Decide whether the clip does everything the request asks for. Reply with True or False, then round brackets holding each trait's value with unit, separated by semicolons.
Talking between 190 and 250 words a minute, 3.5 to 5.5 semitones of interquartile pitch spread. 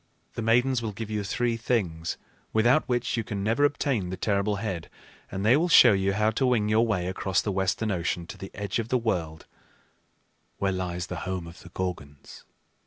True (200 wpm; 3.8 semitones)